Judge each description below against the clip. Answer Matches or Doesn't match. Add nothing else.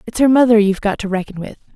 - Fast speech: Matches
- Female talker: Matches